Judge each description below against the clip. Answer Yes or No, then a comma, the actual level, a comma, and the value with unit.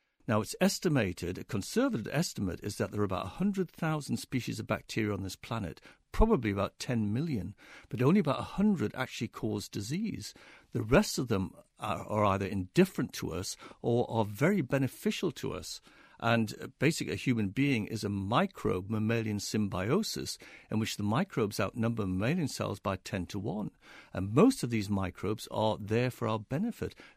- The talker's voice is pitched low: Yes, low, 110 Hz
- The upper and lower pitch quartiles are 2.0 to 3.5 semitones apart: No, wide, 5.5 semitones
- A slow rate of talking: No, average, 170 wpm